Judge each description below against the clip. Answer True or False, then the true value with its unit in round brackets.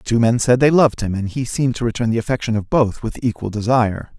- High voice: False (115 Hz)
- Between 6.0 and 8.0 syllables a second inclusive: True (6.3 syllables/s)